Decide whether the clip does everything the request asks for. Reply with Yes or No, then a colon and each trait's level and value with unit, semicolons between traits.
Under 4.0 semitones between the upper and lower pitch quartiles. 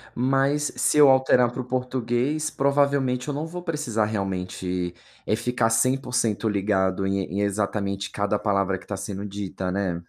No: average, 5.2 semitones